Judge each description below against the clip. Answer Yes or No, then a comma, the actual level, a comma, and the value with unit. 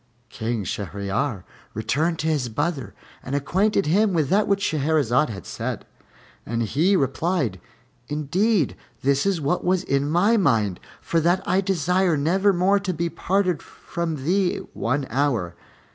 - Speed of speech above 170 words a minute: No, average, 145 wpm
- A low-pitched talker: No, medium, 155 Hz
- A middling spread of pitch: No, wide, 5.9 semitones